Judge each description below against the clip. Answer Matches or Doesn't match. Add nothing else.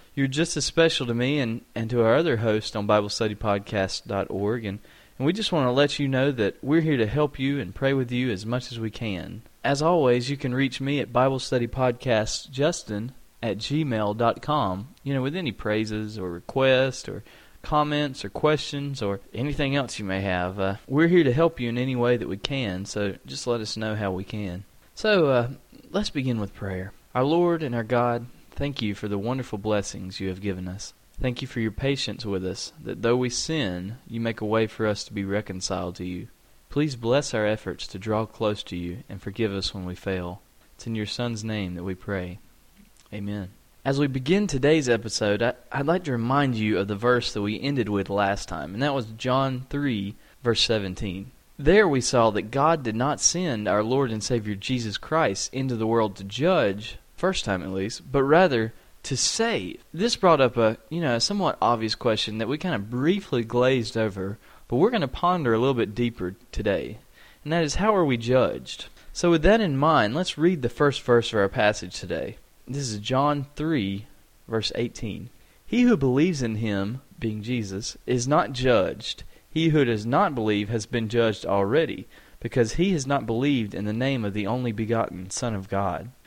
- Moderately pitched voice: Doesn't match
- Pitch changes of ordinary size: Matches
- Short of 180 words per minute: Doesn't match